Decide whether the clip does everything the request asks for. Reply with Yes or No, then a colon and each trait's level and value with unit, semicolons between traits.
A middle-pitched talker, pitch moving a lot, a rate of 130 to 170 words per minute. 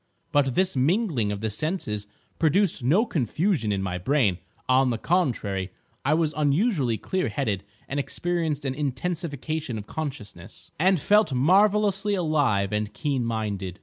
Yes: medium, 145 Hz; wide, 7.8 semitones; average, 145 wpm